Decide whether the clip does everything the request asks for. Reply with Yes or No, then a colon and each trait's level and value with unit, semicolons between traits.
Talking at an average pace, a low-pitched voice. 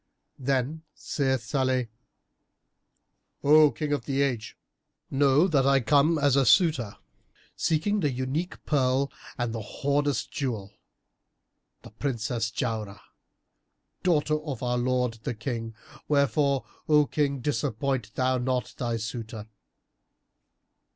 No: slow, 115 wpm; low, 130 Hz